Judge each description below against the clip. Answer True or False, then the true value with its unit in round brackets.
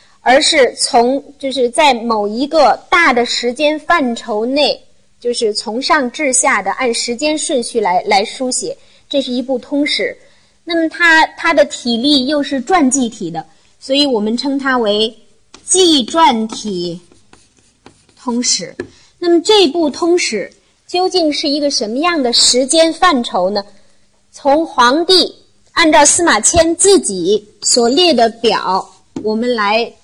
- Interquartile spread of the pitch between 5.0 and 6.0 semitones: True (5.5 semitones)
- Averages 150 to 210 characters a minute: True (200 characters per minute)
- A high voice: True (275 Hz)